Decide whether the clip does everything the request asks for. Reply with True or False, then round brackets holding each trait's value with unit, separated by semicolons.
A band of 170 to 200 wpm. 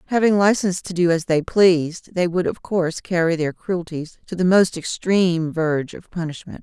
True (190 wpm)